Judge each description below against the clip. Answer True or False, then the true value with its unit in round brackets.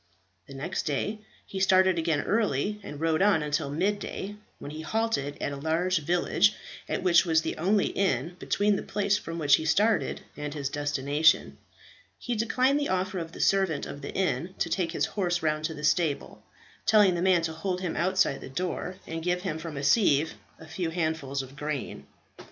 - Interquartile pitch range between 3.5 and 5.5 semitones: True (4.2 semitones)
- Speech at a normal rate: True (195 wpm)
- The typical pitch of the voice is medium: True (170 Hz)